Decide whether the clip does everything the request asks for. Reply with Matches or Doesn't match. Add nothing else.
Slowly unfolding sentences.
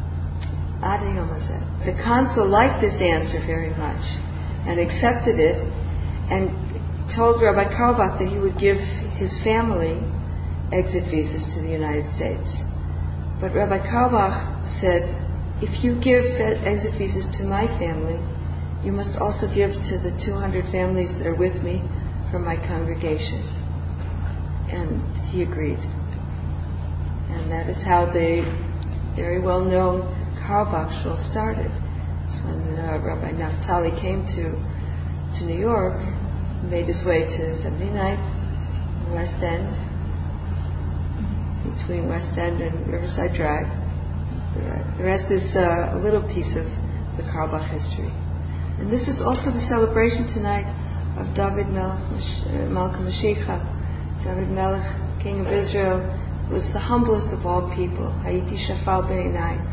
Matches